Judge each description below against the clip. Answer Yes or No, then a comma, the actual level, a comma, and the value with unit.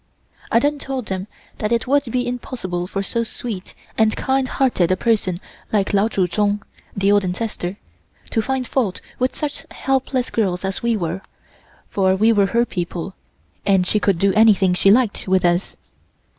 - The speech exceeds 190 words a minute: No, average, 175 wpm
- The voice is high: Yes, high, 210 Hz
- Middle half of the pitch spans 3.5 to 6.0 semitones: Yes, average, 4.2 semitones